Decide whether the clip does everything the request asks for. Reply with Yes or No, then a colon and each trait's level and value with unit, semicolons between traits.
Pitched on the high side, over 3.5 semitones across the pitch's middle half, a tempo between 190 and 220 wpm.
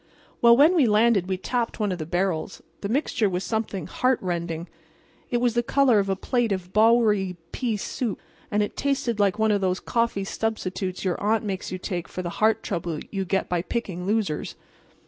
Yes: high, 205 Hz; average, 4.0 semitones; average, 195 wpm